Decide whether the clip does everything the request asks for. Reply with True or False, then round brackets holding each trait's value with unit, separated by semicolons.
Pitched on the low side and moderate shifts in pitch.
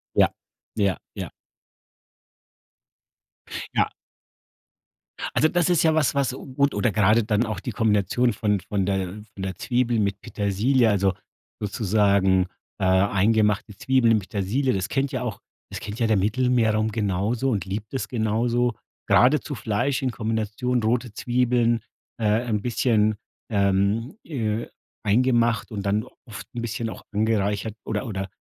True (110 Hz; 3.2 semitones)